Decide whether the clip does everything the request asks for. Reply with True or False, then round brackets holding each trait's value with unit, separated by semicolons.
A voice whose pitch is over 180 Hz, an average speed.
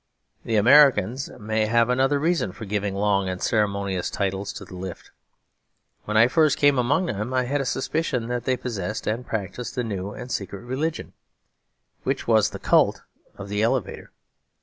False (115 Hz; 170 wpm)